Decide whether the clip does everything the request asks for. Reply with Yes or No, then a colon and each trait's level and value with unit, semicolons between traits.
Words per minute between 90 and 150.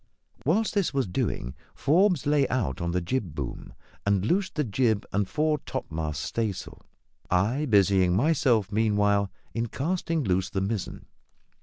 Yes: average, 145 wpm